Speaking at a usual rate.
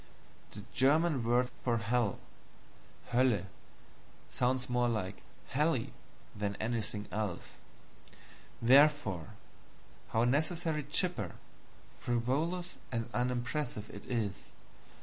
No: slow, 90 wpm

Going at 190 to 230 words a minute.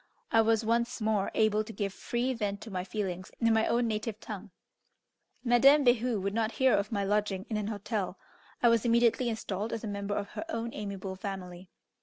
Yes: average, 200 wpm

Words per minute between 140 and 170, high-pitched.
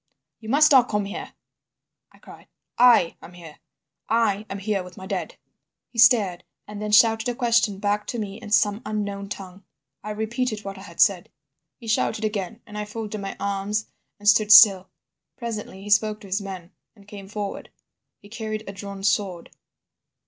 No: average, 180 wpm; high, 210 Hz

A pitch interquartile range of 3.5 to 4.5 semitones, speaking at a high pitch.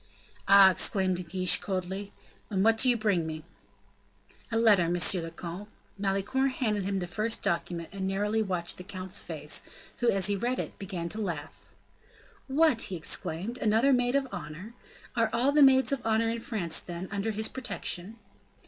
Yes: average, 4.0 semitones; high, 200 Hz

